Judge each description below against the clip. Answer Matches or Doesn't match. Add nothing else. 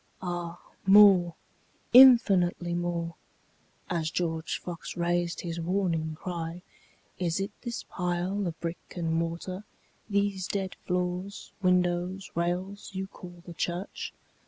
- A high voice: Doesn't match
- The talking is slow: Matches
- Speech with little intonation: Matches